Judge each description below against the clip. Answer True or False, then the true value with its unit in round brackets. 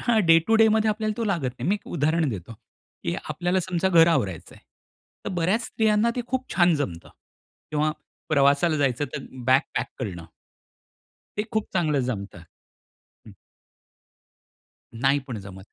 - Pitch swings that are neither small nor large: False (8.1 semitones)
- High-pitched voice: False (160 Hz)